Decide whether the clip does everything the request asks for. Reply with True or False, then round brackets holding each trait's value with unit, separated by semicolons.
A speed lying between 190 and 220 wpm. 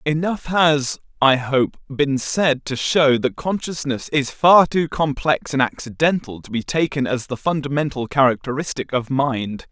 False (155 wpm)